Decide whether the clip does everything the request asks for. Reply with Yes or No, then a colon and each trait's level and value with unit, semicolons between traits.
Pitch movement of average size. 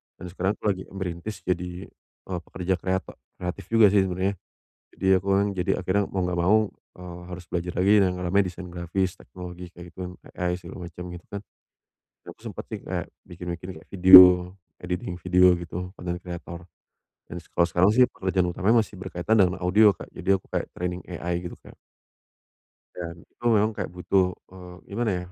No: narrow, 1.4 semitones